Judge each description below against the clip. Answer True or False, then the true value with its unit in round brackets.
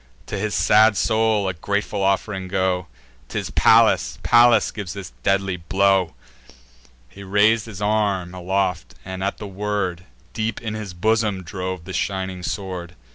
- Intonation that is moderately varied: False (2.2 semitones)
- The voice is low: True (95 Hz)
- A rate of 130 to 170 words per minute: True (145 wpm)